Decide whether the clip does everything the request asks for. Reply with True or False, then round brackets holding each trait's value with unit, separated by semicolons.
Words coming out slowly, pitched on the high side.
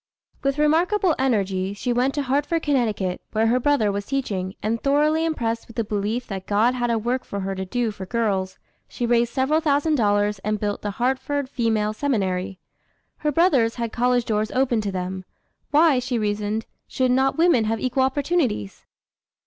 False (180 wpm; 235 Hz)